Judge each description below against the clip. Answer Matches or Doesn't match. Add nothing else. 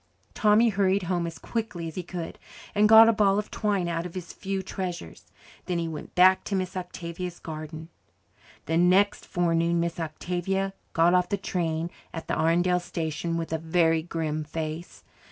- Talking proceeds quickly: Doesn't match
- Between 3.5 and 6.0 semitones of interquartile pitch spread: Doesn't match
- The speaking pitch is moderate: Matches